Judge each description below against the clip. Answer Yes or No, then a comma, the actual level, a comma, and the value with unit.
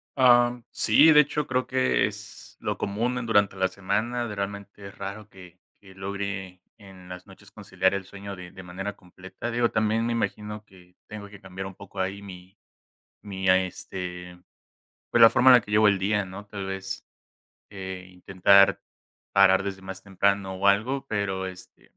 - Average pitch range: No, narrow, 2.2 semitones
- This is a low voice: Yes, low, 100 Hz